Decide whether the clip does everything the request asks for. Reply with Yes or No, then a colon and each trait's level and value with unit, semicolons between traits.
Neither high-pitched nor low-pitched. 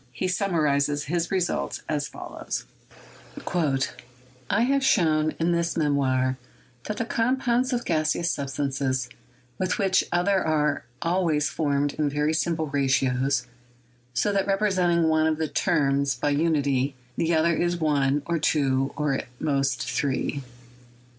Yes: medium, 155 Hz